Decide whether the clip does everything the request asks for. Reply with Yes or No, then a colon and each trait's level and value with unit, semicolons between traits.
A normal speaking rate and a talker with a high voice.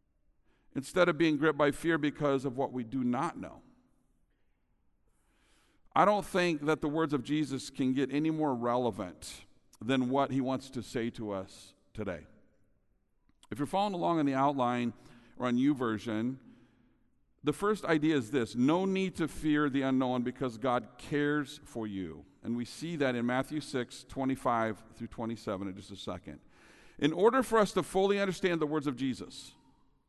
No: average, 170 wpm; low, 135 Hz